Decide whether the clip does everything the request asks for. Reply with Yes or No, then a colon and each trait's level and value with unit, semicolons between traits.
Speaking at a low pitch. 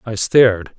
Yes: low, 110 Hz